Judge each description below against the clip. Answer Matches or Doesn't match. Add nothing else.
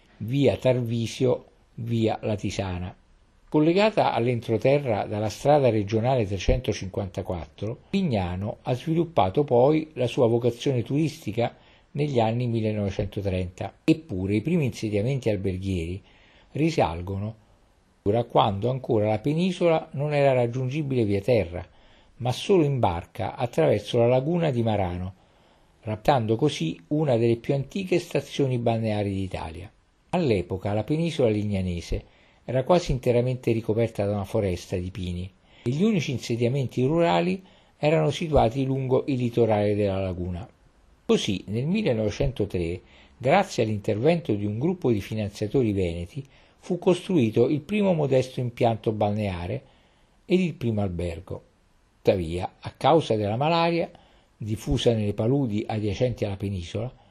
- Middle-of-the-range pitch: Doesn't match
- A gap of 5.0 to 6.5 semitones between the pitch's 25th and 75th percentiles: Matches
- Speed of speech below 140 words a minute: Matches